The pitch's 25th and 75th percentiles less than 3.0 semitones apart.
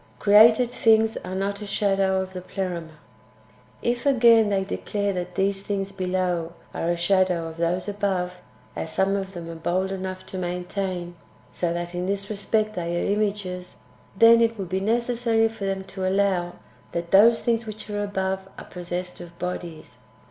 Yes: narrow, 2.5 semitones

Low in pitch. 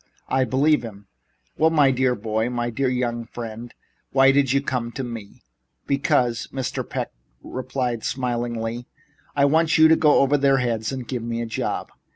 Yes: low, 125 Hz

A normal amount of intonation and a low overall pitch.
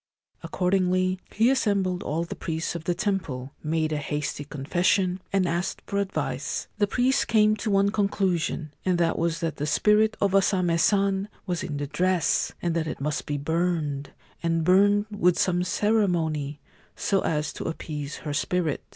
No: average, 4.1 semitones; medium, 175 Hz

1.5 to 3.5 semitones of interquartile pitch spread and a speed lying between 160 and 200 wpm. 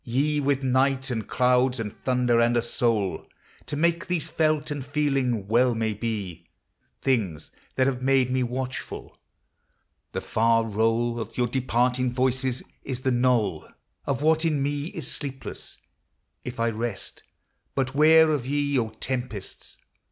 No: average, 2.9 semitones; average, 150 wpm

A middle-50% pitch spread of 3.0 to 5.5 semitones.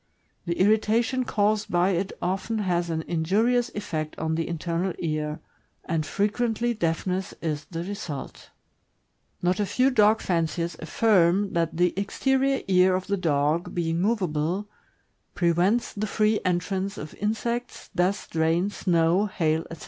Yes: average, 4.0 semitones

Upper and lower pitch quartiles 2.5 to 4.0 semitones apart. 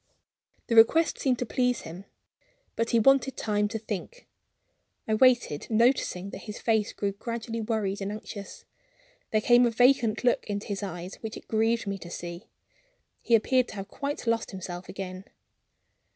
Yes: average, 3.2 semitones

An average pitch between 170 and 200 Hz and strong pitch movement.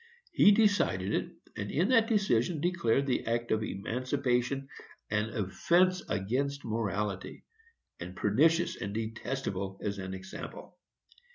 No: low, 115 Hz; wide, 6.2 semitones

